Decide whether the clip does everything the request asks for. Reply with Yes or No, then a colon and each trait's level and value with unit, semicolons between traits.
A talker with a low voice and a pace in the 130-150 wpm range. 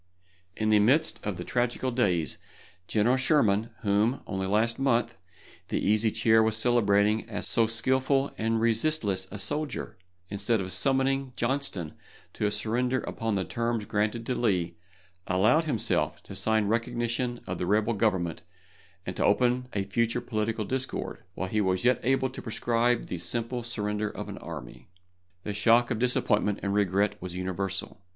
No: low, 110 Hz; average, 160 wpm